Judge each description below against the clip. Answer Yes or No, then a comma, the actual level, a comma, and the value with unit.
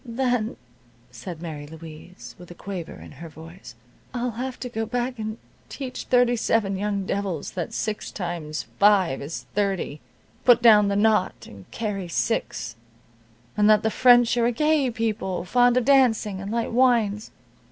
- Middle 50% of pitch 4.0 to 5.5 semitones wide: Yes, average, 5.2 semitones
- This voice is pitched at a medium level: No, high, 210 Hz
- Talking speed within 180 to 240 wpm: No, average, 165 wpm